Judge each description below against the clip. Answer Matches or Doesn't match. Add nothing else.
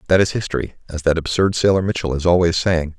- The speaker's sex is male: Matches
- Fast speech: Matches